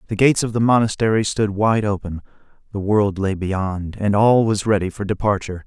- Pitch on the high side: No, low, 105 Hz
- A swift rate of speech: No, average, 190 wpm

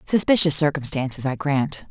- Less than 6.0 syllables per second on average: Yes, 5.1 syllables/s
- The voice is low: No, medium, 145 Hz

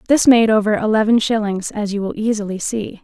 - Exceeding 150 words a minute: Yes, average, 200 wpm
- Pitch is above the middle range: Yes, high, 215 Hz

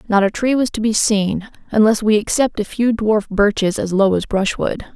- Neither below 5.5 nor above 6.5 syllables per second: No, 4.9 syllables/s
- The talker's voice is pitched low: No, high, 210 Hz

